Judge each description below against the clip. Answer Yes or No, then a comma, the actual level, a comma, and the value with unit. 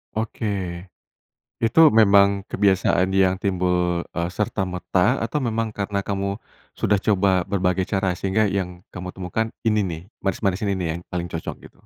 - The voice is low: Yes, very low, 95 Hz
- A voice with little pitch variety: Yes, narrow, 2.1 semitones